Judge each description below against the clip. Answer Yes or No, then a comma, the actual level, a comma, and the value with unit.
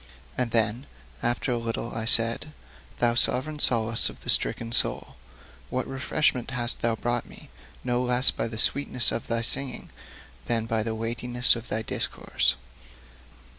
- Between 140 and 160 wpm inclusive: Yes, average, 155 wpm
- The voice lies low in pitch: Yes, low, 120 Hz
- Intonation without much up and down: Yes, narrow, 1.7 semitones